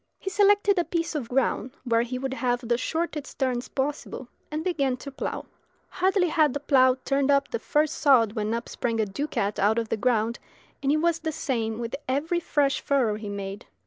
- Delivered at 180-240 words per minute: Yes, fast, 205 wpm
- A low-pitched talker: No, very high, 265 Hz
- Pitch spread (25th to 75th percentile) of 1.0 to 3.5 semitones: No, average, 4.8 semitones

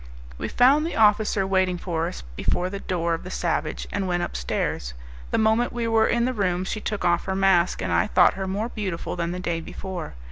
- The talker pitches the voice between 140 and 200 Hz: Yes, high, 190 Hz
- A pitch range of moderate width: Yes, average, 3.8 semitones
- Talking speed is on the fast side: Yes, fast, 220 wpm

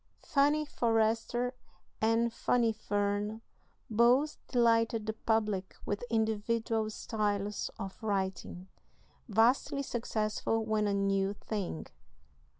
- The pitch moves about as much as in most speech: No, narrow, 2.1 semitones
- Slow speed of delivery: Yes, slow, 95 wpm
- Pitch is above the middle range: Yes, high, 220 Hz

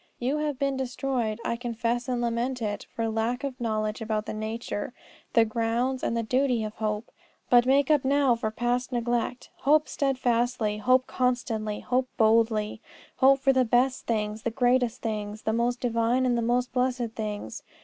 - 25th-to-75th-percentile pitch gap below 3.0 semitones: Yes, narrow, 2.5 semitones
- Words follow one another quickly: No, average, 175 wpm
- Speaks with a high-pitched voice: Yes, high, 240 Hz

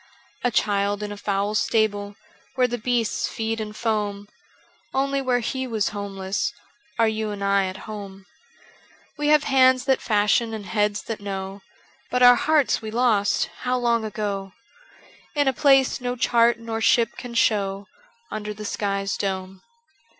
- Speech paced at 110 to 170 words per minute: Yes, average, 165 wpm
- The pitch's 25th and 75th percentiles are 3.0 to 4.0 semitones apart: Yes, average, 3.4 semitones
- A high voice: Yes, high, 215 Hz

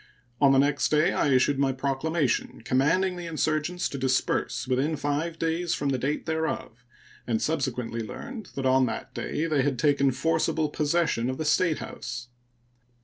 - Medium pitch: Yes, medium, 145 Hz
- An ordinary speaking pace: Yes, average, 160 wpm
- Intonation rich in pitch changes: No, average, 3.5 semitones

